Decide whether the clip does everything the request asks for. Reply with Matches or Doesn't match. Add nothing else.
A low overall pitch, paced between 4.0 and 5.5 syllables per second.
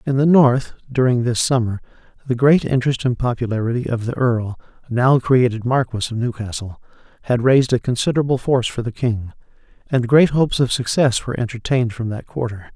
Doesn't match